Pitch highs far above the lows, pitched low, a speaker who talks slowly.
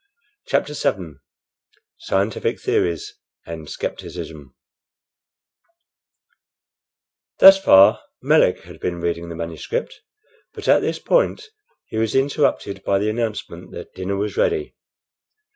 Yes: wide, 7.8 semitones; low, 100 Hz; slow, 110 wpm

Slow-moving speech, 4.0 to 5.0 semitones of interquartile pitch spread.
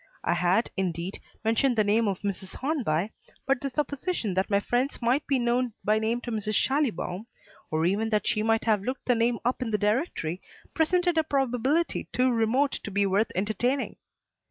No: average, 185 wpm; average, 4.4 semitones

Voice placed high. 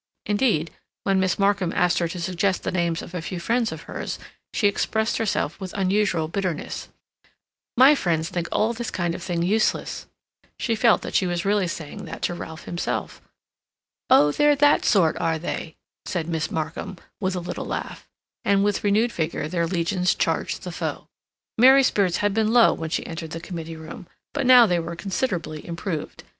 No: medium, 180 Hz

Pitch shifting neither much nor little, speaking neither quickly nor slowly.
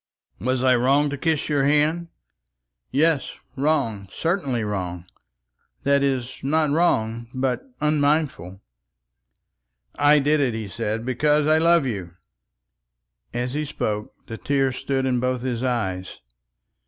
No: average, 4.3 semitones; slow, 130 wpm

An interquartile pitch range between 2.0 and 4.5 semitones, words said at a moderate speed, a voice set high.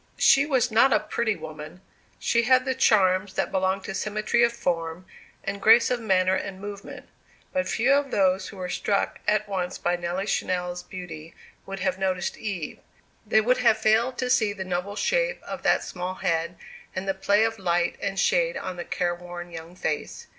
Yes: average, 3.9 semitones; average, 190 wpm; high, 195 Hz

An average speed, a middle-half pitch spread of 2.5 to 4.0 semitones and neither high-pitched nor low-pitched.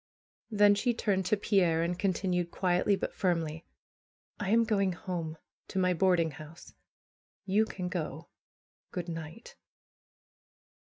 No: slow, 125 wpm; average, 3.2 semitones; medium, 180 Hz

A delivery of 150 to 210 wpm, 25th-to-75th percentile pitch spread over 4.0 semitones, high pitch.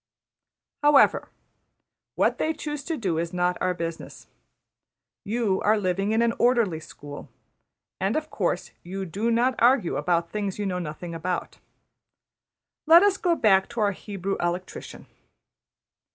No: average, 140 wpm; average, 5.0 semitones; high, 195 Hz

